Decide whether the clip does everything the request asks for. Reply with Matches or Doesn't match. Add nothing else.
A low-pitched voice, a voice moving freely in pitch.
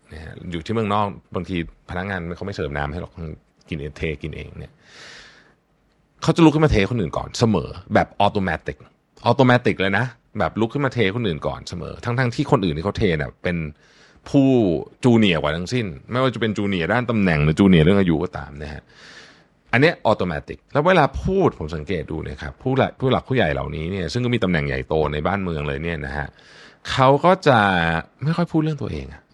Matches